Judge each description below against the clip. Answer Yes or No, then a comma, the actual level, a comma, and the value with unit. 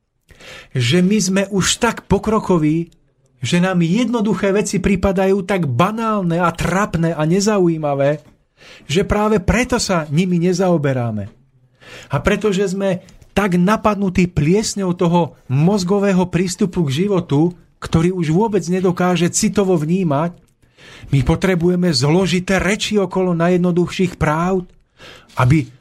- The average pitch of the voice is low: No, medium, 180 Hz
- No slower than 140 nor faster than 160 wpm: No, slow, 110 wpm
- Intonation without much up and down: No, average, 3.6 semitones